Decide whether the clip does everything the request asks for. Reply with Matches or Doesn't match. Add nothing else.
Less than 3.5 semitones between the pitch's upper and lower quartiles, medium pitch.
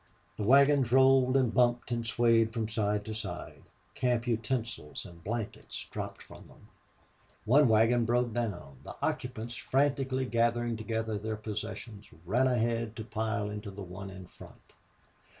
Doesn't match